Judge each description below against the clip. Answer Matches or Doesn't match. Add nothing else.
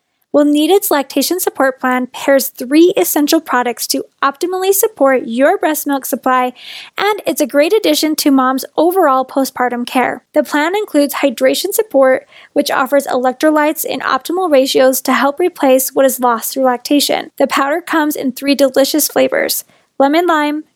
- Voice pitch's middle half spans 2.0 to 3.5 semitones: Matches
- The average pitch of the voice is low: Doesn't match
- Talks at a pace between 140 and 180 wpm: Matches